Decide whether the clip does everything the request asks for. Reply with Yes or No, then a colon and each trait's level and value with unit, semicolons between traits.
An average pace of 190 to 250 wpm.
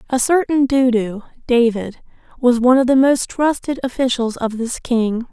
No: average, 160 wpm